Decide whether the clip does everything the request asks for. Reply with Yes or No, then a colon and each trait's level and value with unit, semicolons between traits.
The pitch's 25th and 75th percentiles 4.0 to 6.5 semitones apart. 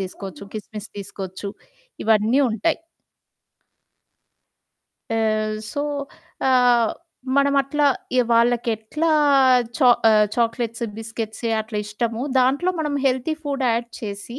No: average, 3.3 semitones